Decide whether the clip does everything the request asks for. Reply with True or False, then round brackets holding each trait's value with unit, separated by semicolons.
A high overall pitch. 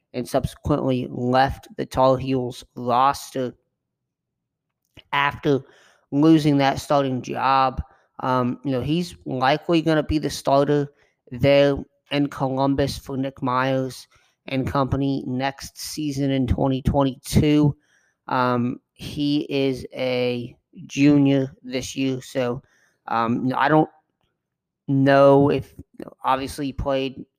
False (135 Hz)